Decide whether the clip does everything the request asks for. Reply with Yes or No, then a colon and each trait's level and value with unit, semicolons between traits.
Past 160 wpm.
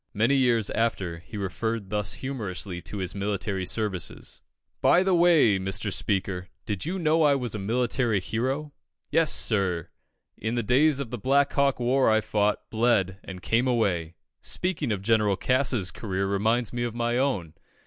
Yes: average, 170 wpm